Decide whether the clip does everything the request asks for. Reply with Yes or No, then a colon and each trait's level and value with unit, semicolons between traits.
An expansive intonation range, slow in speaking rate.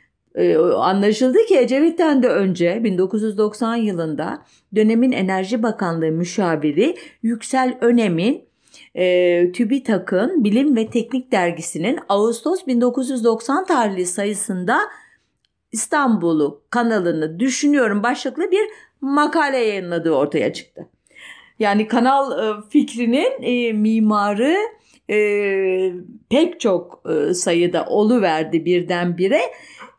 Yes: wide, 5.7 semitones; slow, 80 wpm